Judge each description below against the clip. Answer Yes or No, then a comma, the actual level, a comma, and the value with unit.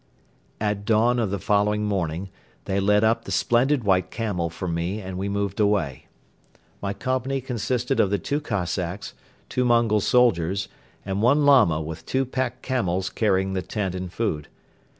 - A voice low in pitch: Yes, low, 105 Hz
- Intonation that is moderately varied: Yes, average, 4.2 semitones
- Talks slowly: No, average, 165 wpm